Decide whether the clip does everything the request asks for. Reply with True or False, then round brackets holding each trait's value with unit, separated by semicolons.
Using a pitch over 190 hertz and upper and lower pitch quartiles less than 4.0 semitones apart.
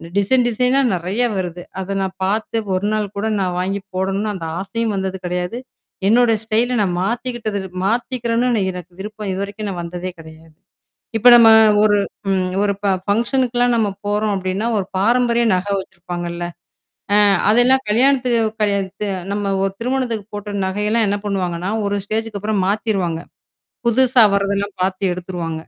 True (205 Hz; 3.5 semitones)